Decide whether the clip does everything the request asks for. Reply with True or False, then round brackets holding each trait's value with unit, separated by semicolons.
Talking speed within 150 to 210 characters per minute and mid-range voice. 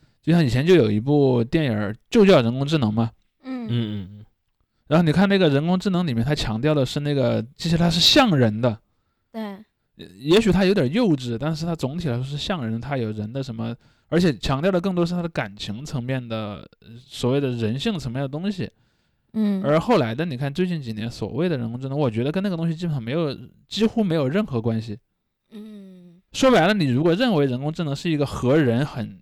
False (315 characters per minute; 145 Hz)